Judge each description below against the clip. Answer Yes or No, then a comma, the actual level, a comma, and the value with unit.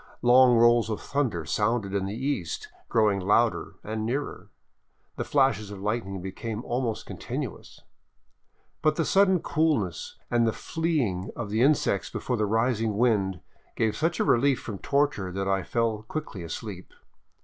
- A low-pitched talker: Yes, low, 115 Hz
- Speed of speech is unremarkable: Yes, average, 150 wpm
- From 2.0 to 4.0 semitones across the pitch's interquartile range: No, average, 4.6 semitones